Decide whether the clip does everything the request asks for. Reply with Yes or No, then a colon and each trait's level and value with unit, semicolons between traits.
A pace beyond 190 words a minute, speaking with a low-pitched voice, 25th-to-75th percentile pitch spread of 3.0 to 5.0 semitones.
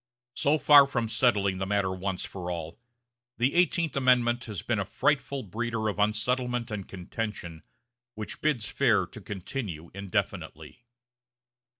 No: slow, 135 wpm; low, 110 Hz; average, 4.6 semitones